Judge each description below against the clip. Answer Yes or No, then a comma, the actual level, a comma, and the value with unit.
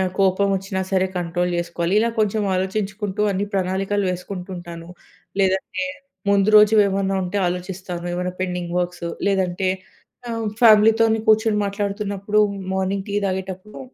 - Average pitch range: No, narrow, 2.2 semitones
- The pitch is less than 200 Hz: Yes, high, 190 Hz